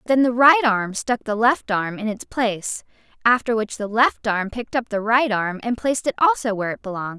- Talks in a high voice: Yes, high, 225 Hz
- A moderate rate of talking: No, fast, 235 wpm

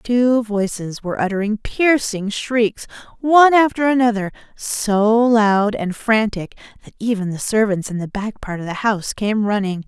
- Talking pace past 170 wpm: No, average, 160 wpm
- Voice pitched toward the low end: No, high, 215 Hz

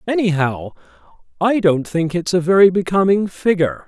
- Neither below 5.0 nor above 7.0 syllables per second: Yes, 5.2 syllables/s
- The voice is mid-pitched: Yes, medium, 175 Hz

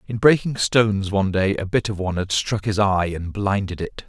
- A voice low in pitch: Yes, low, 100 Hz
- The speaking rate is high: Yes, fast, 235 wpm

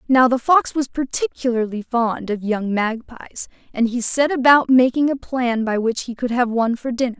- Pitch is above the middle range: Yes, high, 245 Hz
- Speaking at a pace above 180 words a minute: Yes, average, 200 wpm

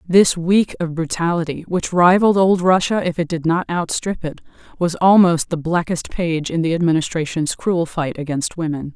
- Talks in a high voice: No, medium, 170 Hz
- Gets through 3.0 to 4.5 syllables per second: No, 4.9 syllables/s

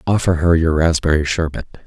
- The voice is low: Yes, very low, 80 Hz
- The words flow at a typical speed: Yes, average, 160 wpm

